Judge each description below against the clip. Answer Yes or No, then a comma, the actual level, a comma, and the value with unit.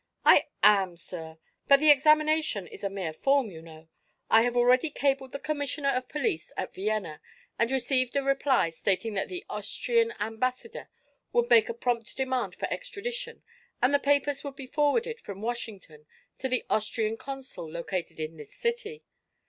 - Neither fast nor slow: Yes, average, 165 wpm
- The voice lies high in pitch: Yes, very high, 250 Hz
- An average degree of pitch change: No, wide, 6.1 semitones